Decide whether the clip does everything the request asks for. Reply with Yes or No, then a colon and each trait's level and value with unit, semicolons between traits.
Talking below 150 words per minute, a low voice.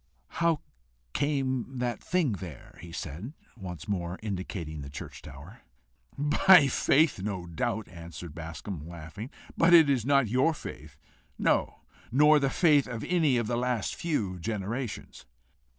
Yes: slow, 135 wpm; low, 115 Hz